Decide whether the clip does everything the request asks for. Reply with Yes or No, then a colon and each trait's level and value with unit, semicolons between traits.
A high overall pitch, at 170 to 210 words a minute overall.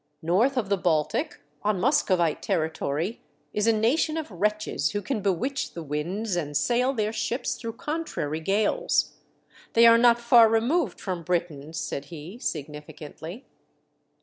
No: high, 205 Hz; average, 145 wpm